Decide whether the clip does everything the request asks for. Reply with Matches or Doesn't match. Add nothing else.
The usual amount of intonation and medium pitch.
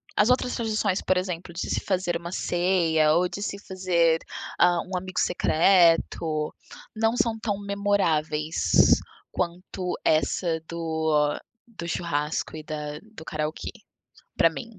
Matches